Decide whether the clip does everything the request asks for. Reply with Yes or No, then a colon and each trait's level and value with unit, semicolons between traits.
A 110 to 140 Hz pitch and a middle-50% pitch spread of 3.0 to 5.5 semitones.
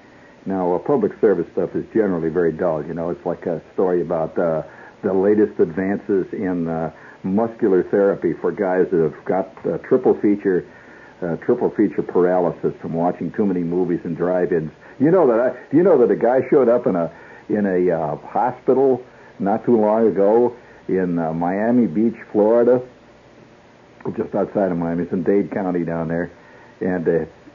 No: very low, 95 Hz; average, 4.0 semitones